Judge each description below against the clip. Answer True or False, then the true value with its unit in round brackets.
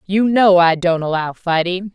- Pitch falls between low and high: True (180 Hz)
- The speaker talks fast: False (185 wpm)